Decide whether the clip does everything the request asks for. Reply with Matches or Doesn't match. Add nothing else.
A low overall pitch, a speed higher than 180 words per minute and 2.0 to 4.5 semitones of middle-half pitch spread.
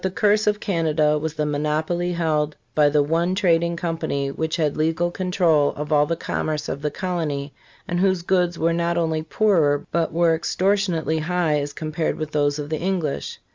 Doesn't match